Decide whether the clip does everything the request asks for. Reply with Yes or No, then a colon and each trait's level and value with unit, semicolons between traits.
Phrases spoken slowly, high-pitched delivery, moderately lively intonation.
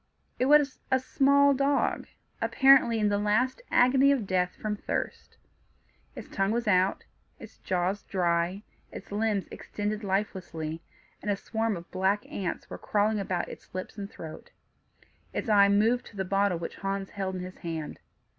No: average, 165 wpm; high, 205 Hz; average, 3.4 semitones